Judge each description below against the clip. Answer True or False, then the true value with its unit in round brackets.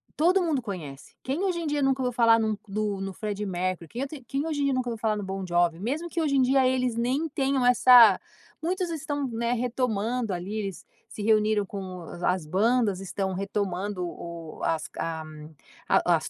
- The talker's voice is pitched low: False (225 Hz)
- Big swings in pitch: True (5.7 semitones)